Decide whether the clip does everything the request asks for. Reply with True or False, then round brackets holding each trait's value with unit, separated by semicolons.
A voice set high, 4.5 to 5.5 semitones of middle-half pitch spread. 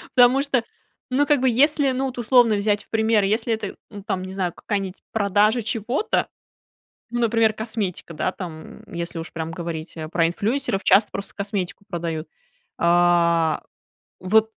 True (205 Hz; 4.9 semitones)